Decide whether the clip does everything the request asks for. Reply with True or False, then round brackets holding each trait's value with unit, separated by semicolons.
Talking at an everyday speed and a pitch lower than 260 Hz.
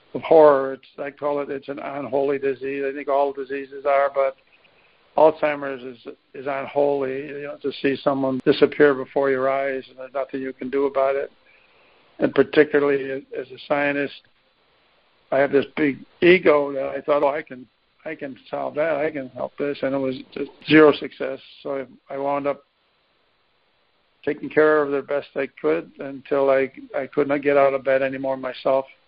True (180 wpm; 140 Hz)